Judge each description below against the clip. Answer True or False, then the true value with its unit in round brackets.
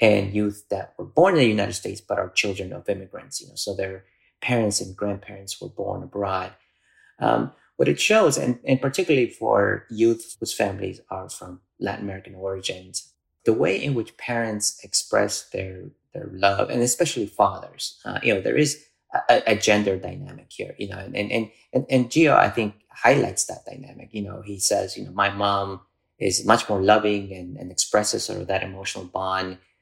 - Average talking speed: True (190 wpm)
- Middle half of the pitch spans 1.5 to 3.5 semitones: True (2.8 semitones)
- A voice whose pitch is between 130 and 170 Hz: False (100 Hz)